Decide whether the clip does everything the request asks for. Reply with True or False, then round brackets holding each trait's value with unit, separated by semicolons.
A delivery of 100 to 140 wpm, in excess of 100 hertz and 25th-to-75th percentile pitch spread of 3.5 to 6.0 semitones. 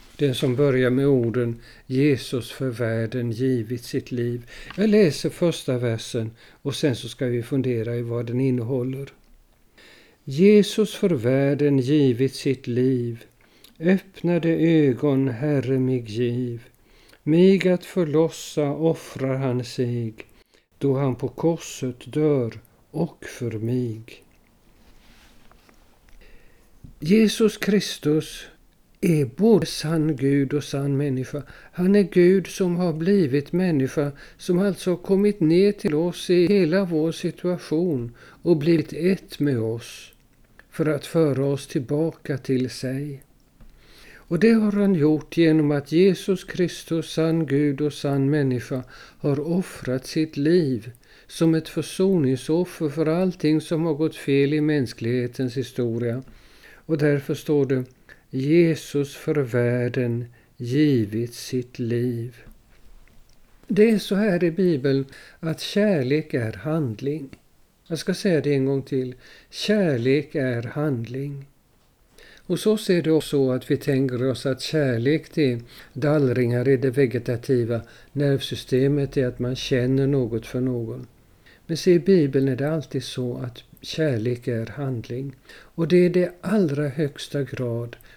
True (135 wpm; 140 Hz; 4.5 semitones)